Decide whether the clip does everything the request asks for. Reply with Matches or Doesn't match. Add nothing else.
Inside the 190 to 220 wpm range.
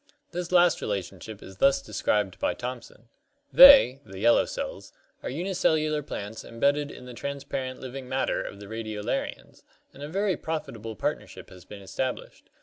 Doesn't match